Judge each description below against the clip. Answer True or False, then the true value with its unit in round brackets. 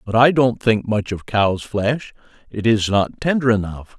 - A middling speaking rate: True (195 wpm)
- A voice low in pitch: True (110 Hz)